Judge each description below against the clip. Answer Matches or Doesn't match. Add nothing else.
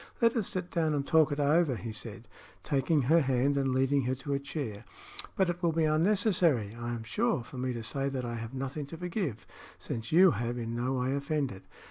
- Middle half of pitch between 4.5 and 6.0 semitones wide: Matches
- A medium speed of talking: Doesn't match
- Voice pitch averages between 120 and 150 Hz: Matches